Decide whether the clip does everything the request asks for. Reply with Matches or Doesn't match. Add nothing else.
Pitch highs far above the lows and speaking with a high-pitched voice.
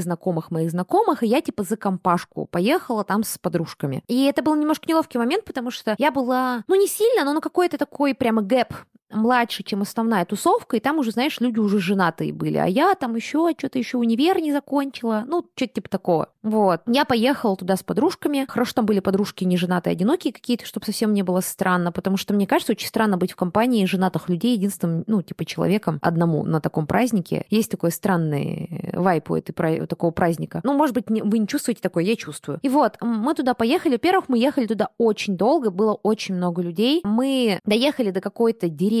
Matches